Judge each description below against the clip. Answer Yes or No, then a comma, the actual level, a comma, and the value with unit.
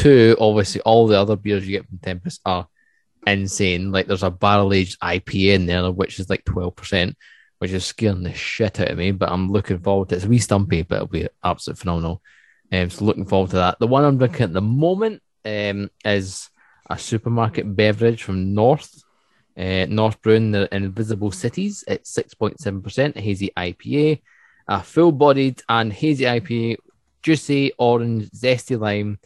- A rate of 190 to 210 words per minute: No, average, 180 wpm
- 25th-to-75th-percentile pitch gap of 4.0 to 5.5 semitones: No, average, 3.5 semitones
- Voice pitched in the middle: No, low, 105 Hz